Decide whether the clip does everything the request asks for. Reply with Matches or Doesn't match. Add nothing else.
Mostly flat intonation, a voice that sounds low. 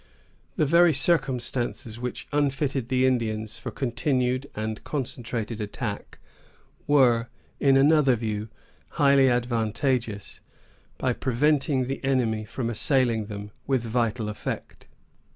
Doesn't match